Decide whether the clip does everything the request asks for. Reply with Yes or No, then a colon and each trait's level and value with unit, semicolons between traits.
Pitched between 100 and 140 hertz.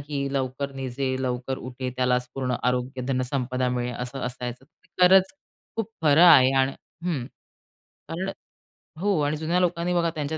Yes: low, 135 Hz